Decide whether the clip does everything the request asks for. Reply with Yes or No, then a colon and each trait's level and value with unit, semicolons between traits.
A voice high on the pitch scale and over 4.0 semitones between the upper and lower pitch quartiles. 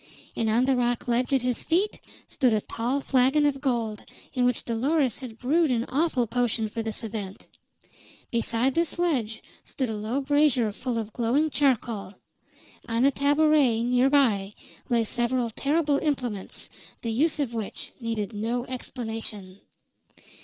No: high, 245 Hz; average, 3.5 semitones